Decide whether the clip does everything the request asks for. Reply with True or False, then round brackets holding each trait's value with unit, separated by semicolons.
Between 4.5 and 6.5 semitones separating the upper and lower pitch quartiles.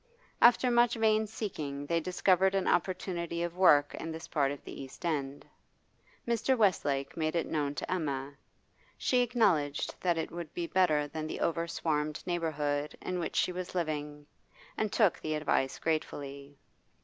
False (4.0 semitones)